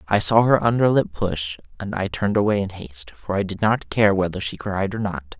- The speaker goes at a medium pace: No, fast, 245 wpm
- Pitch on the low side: Yes, low, 100 Hz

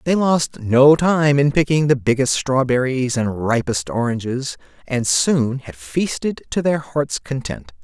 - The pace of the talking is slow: No, average, 155 wpm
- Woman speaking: No, male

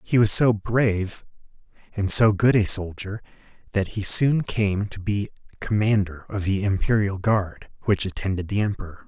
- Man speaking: Yes, male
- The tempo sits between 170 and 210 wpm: No, average, 160 wpm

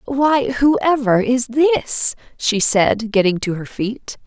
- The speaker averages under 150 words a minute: Yes, average, 140 wpm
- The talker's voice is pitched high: Yes, high, 240 Hz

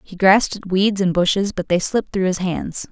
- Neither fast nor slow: No, fast, 245 wpm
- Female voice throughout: Yes, female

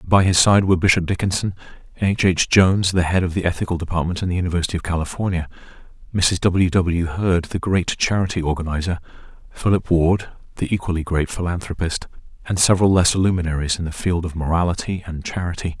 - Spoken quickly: No, average, 170 wpm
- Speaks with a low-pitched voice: Yes, very low, 90 Hz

